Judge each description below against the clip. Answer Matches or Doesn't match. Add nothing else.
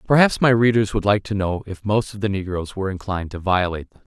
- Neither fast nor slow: Doesn't match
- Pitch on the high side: Doesn't match